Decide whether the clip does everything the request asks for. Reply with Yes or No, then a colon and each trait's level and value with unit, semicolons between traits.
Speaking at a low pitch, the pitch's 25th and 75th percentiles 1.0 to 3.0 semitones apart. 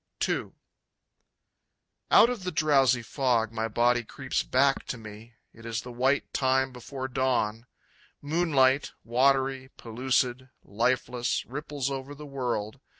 Yes: low, 130 Hz; narrow, 2.5 semitones